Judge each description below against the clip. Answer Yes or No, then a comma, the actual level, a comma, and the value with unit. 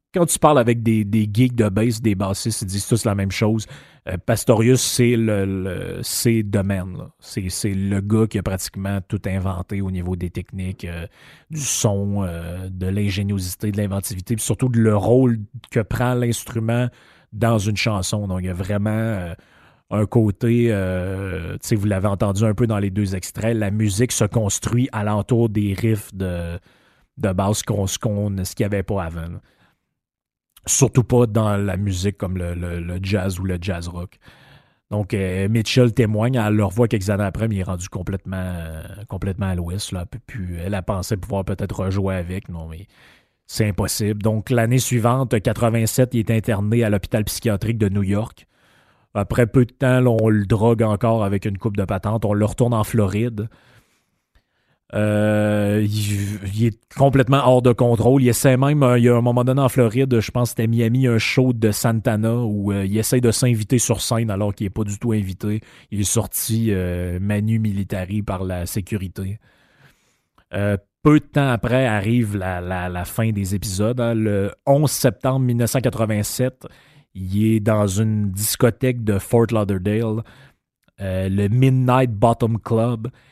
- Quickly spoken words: No, average, 185 wpm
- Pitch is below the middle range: Yes, low, 105 Hz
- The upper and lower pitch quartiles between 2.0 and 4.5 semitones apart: Yes, average, 3.1 semitones